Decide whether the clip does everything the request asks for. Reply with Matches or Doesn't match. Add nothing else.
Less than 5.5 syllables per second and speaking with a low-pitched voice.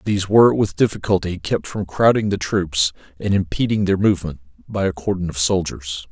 Doesn't match